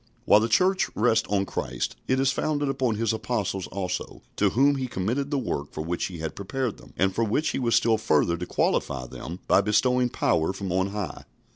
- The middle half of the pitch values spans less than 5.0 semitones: No, wide, 5.5 semitones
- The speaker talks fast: Yes, fast, 215 wpm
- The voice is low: Yes, low, 110 Hz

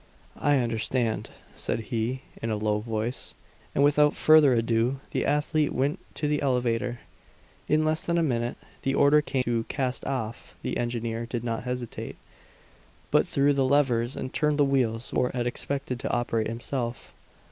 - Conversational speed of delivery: Yes, average, 170 wpm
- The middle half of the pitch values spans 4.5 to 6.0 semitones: No, average, 3.4 semitones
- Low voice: Yes, low, 125 Hz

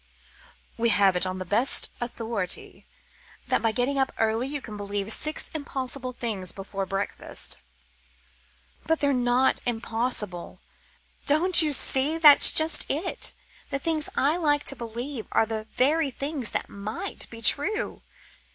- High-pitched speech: Yes, high, 245 Hz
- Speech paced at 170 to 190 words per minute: No, average, 140 wpm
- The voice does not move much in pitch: No, average, 4.9 semitones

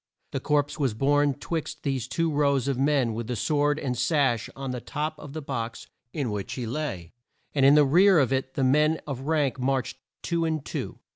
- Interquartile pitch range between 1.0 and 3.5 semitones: Yes, average, 2.7 semitones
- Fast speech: Yes, fast, 210 wpm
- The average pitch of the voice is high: No, medium, 140 Hz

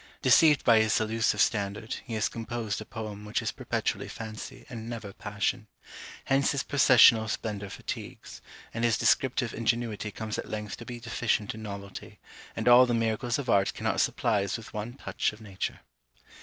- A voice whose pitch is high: No, low, 110 Hz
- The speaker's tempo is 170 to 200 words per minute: Yes, average, 175 wpm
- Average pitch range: No, narrow, 2.0 semitones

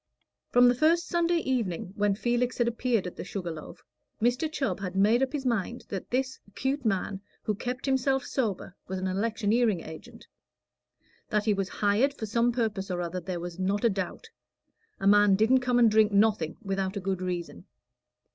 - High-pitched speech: Yes, high, 215 Hz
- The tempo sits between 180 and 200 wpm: Yes, average, 185 wpm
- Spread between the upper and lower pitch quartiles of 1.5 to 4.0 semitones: No, average, 4.4 semitones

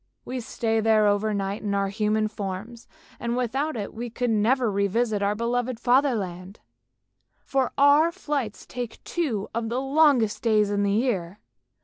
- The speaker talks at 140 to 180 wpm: Yes, average, 155 wpm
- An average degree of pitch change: Yes, average, 3.4 semitones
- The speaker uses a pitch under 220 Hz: No, high, 225 Hz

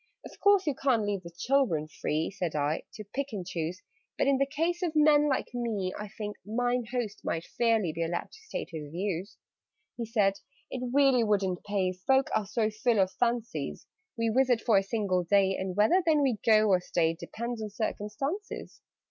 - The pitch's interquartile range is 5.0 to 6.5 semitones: Yes, average, 5.3 semitones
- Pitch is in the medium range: No, high, 215 Hz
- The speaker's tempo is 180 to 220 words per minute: Yes, average, 190 wpm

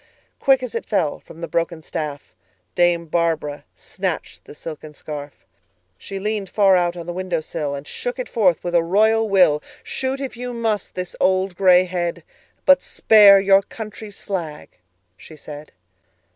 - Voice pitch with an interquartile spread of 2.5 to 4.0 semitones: No, average, 4.9 semitones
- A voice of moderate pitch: Yes, medium, 180 Hz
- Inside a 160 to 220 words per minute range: No, average, 145 wpm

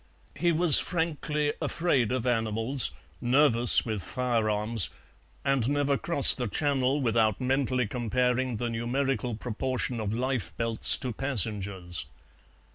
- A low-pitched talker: Yes, low, 125 Hz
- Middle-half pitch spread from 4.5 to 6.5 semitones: No, average, 3.4 semitones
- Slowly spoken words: Yes, slow, 115 wpm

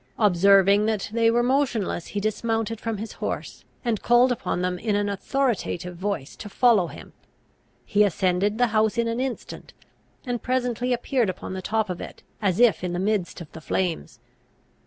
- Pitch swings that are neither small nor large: Yes, average, 3.9 semitones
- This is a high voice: Yes, high, 215 Hz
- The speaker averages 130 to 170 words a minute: No, average, 180 wpm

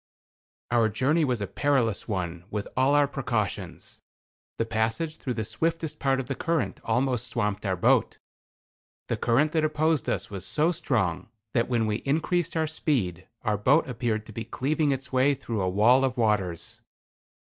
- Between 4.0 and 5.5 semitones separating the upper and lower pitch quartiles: Yes, average, 5.1 semitones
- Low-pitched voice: Yes, low, 125 Hz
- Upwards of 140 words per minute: Yes, average, 170 wpm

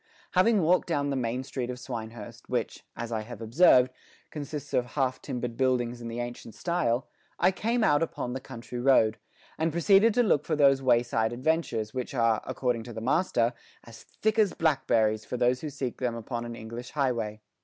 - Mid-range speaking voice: No, low, 125 Hz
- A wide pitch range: No, average, 4.2 semitones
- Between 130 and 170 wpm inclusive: No, average, 190 wpm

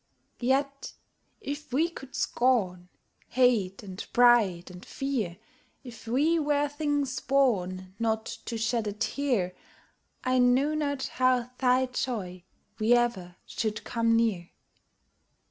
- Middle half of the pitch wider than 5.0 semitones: No, average, 4.6 semitones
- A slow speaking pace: Yes, slow, 120 wpm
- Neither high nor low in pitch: No, high, 245 Hz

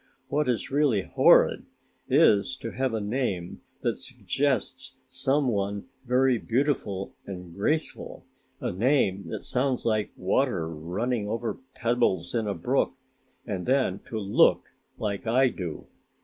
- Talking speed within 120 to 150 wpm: Yes, slow, 135 wpm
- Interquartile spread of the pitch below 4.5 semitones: No, average, 5.0 semitones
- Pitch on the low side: Yes, low, 115 Hz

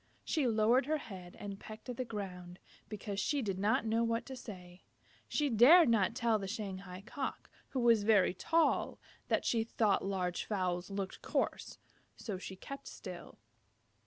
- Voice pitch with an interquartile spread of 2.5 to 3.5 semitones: No, average, 3.9 semitones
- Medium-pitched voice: No, high, 210 Hz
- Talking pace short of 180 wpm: Yes, average, 165 wpm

